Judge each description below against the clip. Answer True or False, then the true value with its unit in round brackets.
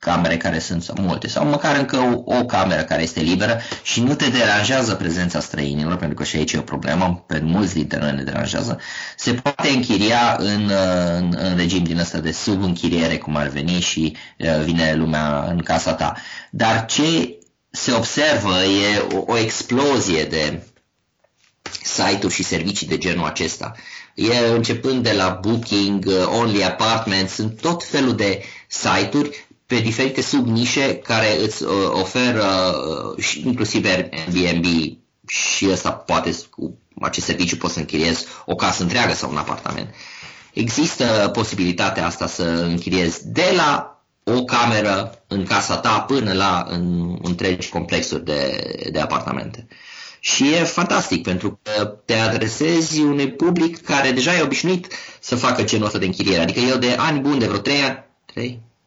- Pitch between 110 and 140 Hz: False (100 Hz)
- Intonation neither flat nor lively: False (5.9 semitones)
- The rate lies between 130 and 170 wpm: True (155 wpm)